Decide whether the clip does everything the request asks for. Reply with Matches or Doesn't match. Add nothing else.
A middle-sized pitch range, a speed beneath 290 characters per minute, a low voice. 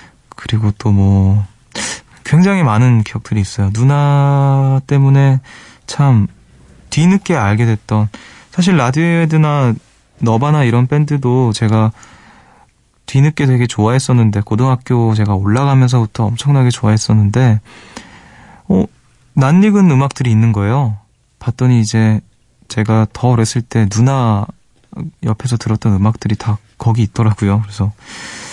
Matches